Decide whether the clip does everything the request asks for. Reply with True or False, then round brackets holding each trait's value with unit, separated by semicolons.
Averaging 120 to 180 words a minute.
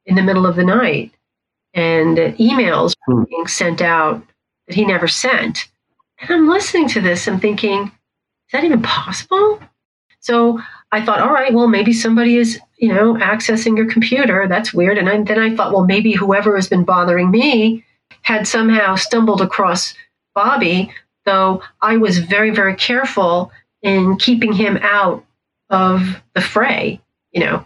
True (165 wpm)